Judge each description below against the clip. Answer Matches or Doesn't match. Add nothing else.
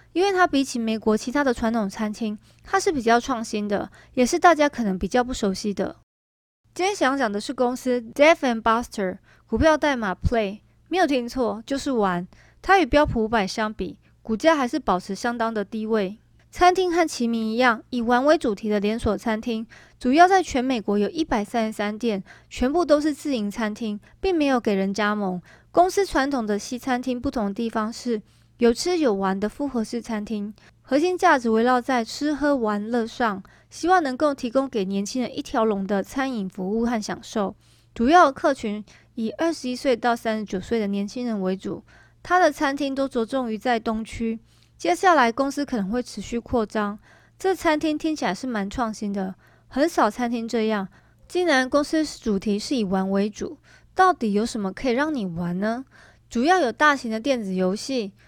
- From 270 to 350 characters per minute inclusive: Matches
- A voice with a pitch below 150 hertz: Doesn't match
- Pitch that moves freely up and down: Doesn't match